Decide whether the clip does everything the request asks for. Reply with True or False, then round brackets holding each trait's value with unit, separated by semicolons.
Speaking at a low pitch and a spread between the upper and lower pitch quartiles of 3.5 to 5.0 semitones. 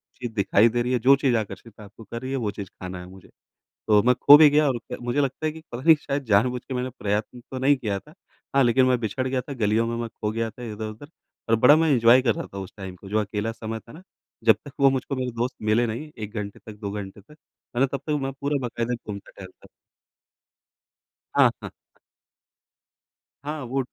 True (120 Hz; 3.8 semitones)